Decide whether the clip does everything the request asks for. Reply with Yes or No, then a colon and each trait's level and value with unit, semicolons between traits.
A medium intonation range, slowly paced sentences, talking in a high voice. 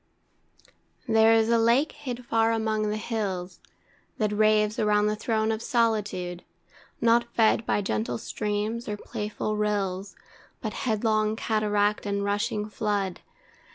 No: narrow, 1.4 semitones; slow, 130 wpm; high, 215 Hz